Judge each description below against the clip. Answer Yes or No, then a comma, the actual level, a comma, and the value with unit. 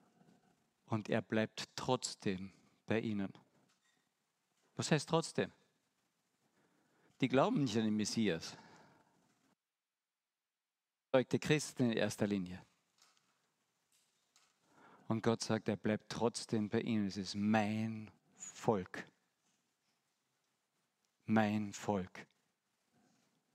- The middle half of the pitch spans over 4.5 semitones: No, average, 3.5 semitones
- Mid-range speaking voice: No, low, 110 Hz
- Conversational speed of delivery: No, slow, 85 wpm